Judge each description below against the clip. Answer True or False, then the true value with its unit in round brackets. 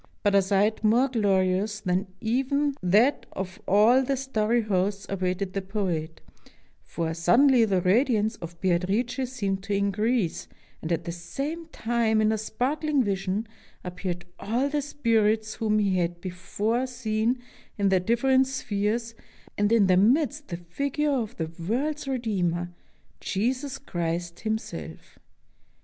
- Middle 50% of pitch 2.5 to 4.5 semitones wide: False (4.9 semitones)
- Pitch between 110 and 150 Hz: False (215 Hz)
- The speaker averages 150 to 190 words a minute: False (140 wpm)